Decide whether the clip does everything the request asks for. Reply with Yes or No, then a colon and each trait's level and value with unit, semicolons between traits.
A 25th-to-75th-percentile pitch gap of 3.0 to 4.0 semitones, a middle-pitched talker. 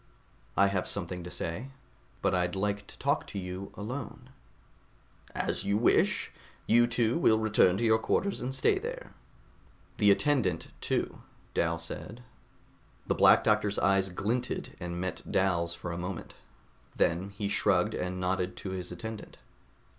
No: average, 3.5 semitones; low, 100 Hz